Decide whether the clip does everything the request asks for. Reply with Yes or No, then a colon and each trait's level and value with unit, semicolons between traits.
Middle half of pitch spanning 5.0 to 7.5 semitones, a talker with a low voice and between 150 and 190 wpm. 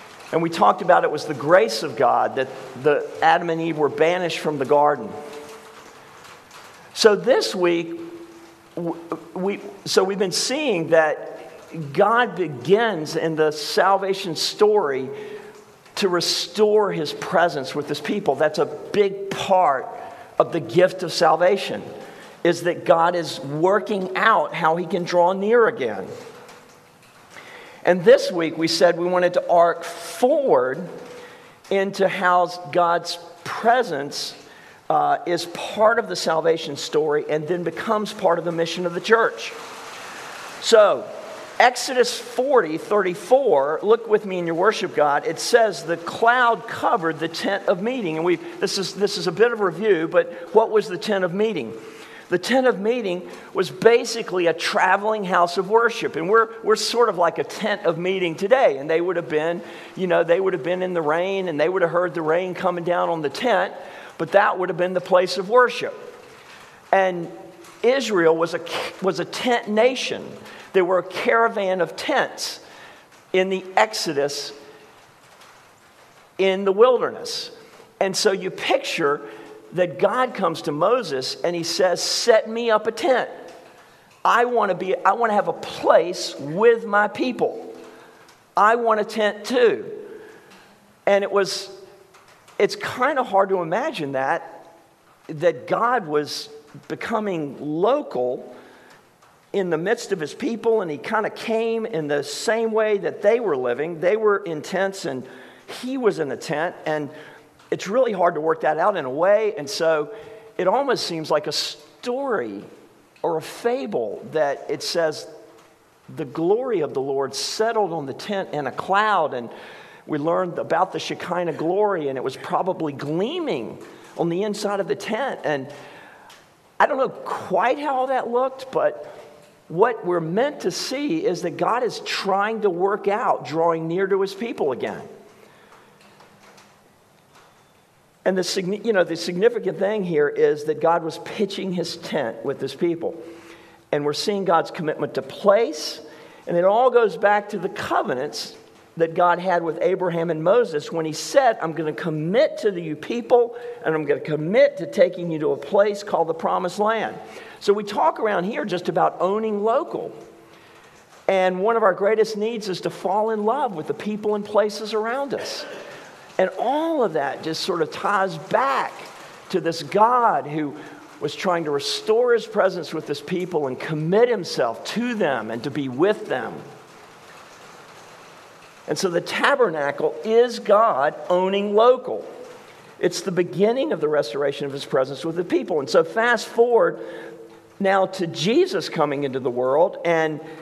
No: wide, 5.4 semitones; medium, 185 Hz; average, 165 wpm